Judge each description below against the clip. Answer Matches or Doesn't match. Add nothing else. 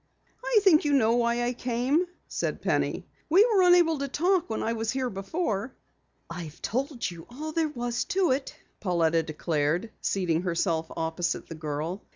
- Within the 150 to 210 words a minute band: Matches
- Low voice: Doesn't match